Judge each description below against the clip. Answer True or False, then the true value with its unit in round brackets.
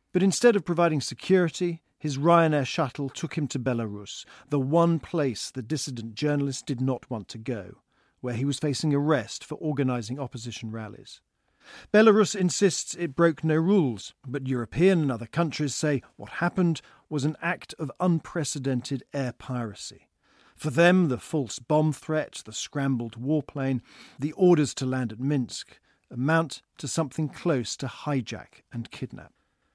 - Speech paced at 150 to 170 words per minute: True (155 wpm)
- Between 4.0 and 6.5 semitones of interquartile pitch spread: True (4.3 semitones)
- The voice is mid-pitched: True (145 Hz)